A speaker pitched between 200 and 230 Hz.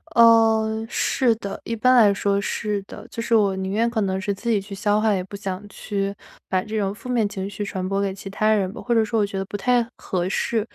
Yes: high, 205 Hz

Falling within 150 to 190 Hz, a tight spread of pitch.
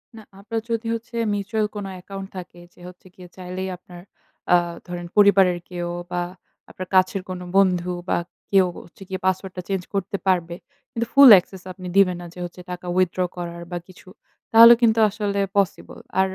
Yes: medium, 185 Hz; narrow, 2.1 semitones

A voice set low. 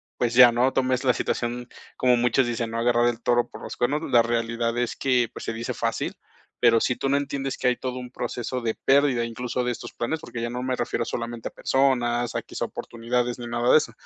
Yes: low, 120 Hz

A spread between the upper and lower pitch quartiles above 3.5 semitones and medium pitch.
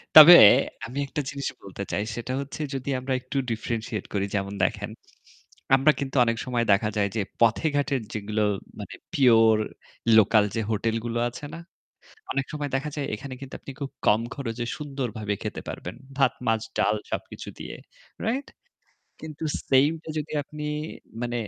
No: average, 4.2 semitones; low, 125 Hz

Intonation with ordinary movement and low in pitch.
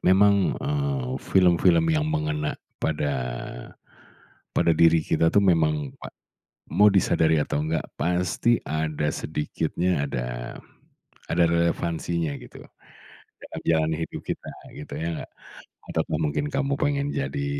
Yes: average, 3.7 semitones; very low, 80 Hz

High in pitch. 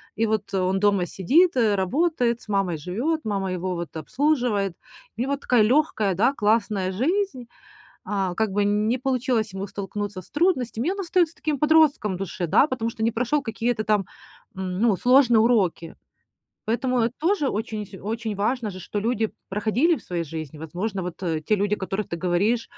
Yes: high, 215 Hz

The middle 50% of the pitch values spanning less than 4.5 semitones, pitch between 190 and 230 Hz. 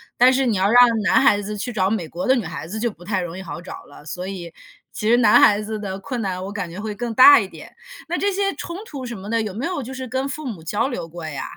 No: average, 5.1 semitones; high, 210 Hz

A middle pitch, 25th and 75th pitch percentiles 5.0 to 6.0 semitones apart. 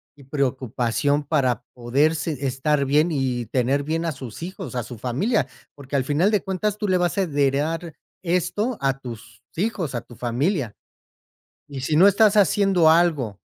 Yes: medium, 145 Hz; average, 5.3 semitones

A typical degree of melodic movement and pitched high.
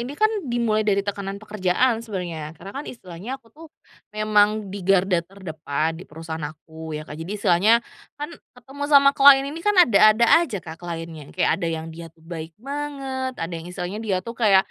No: wide, 6.3 semitones; high, 200 Hz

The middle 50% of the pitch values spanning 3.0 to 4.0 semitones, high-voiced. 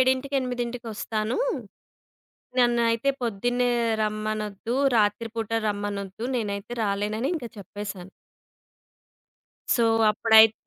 No: narrow, 2.6 semitones; high, 220 Hz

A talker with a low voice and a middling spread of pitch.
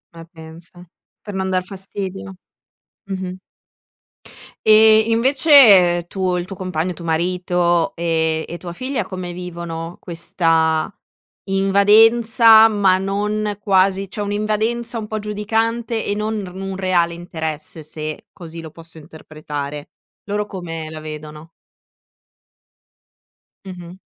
No: medium, 185 Hz; average, 3.9 semitones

